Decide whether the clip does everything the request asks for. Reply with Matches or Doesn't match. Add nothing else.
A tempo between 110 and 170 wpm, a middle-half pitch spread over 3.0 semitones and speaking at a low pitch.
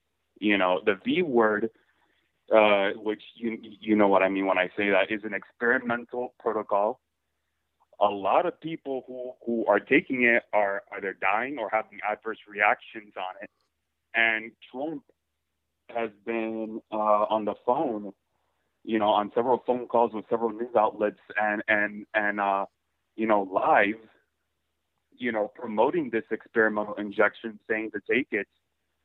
Matches